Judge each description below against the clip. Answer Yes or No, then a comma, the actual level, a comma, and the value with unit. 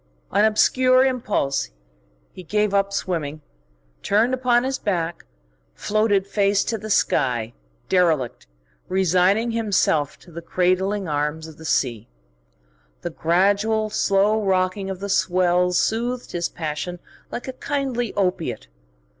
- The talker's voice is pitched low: No, high, 195 Hz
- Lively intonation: No, average, 4.2 semitones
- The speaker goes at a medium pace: No, slow, 125 wpm